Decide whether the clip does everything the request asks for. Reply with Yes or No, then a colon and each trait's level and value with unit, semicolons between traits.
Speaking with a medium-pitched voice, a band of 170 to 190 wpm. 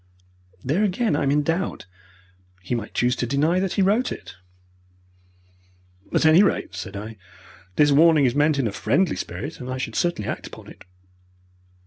Yes: medium, 145 Hz; average, 175 wpm